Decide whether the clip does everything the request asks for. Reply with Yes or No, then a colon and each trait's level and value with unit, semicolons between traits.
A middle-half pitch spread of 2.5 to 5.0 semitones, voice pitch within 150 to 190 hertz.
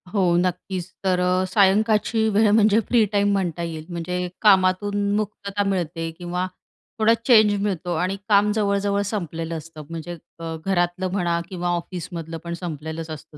Yes: average, 3.1 semitones; medium, 185 Hz